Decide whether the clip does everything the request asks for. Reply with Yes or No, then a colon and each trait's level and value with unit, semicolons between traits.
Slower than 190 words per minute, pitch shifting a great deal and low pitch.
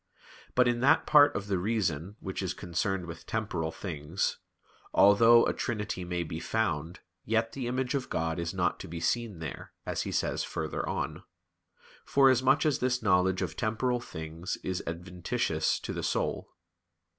Yes: average, 165 wpm; wide, 5.9 semitones; very low, 95 Hz